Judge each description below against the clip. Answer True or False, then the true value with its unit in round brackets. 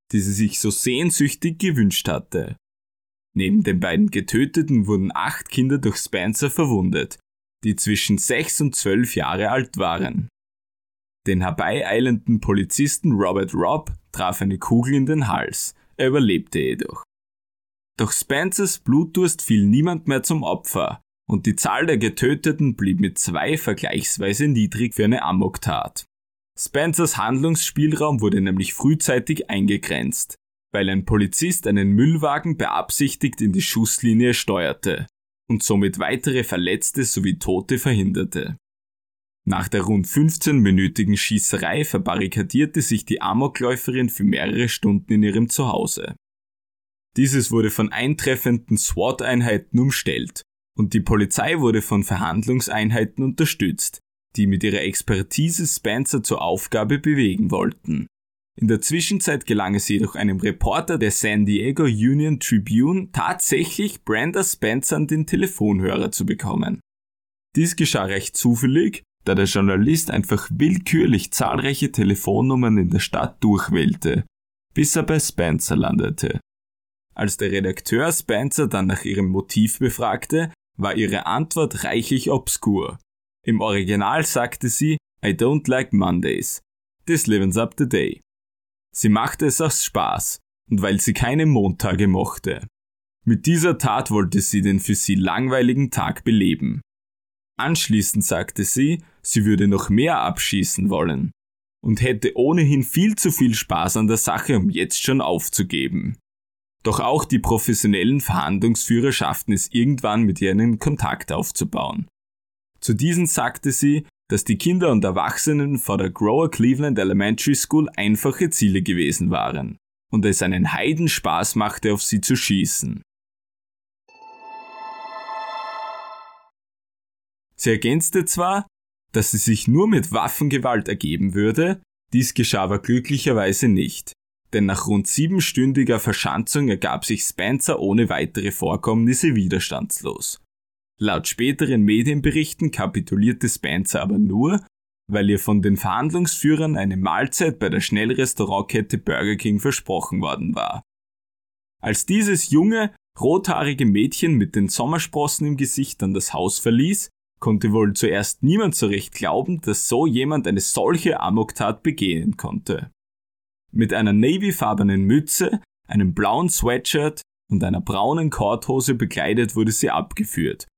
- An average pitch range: False (6.8 semitones)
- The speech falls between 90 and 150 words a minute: True (130 wpm)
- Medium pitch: False (115 Hz)